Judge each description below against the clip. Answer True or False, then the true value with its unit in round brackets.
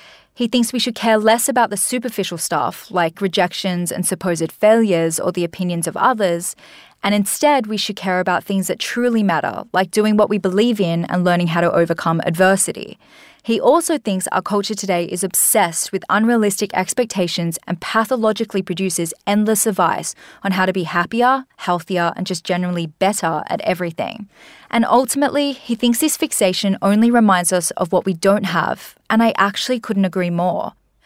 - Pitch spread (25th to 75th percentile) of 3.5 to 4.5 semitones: True (4.1 semitones)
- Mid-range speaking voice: False (195 Hz)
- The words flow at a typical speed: True (175 wpm)